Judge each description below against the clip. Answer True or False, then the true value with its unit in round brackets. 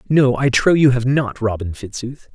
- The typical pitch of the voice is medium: False (125 Hz)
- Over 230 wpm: False (205 wpm)